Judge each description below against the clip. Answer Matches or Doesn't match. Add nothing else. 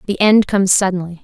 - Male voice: Doesn't match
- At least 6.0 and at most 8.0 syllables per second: Matches